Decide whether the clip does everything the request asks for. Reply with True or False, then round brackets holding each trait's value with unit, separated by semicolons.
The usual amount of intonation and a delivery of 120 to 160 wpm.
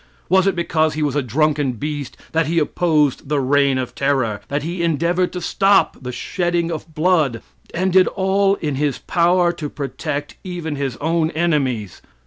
False (3.6 semitones; 180 wpm)